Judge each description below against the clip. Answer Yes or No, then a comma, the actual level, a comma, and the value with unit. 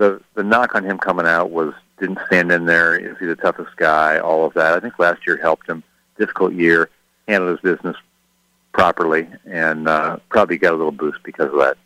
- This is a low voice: Yes, very low, 85 Hz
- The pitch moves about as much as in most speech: No, narrow, 1.7 semitones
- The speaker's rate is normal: No, fast, 215 wpm